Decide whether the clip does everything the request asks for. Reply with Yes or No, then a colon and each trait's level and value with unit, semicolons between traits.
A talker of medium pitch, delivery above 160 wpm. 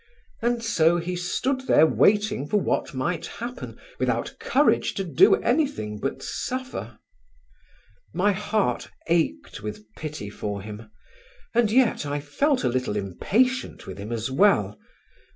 No: medium, 170 Hz; slow, 135 wpm